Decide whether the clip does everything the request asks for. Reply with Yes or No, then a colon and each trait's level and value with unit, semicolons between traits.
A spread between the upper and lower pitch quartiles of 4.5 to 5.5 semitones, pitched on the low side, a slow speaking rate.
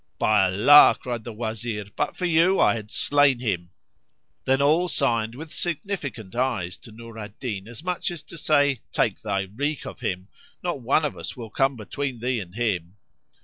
No: average, 5.1 semitones; low, 120 Hz; average, 190 wpm